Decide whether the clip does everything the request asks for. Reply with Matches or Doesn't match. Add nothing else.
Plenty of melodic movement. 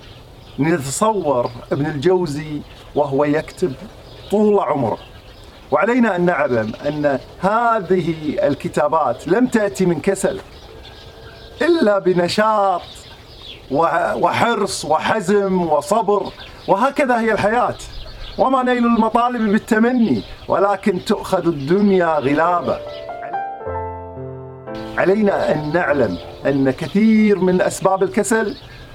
Matches